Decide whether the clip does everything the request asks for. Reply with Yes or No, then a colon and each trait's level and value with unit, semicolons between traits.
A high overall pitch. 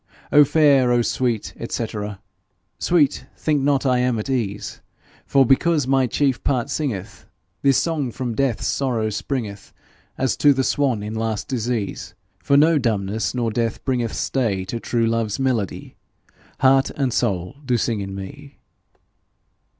No: low, 125 Hz